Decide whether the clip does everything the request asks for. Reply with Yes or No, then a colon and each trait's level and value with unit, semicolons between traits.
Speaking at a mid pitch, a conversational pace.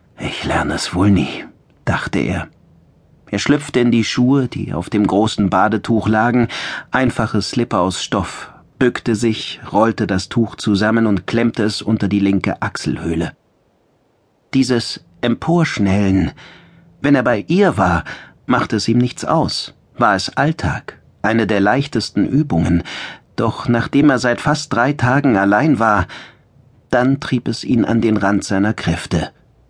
No: low, 110 Hz; average, 145 wpm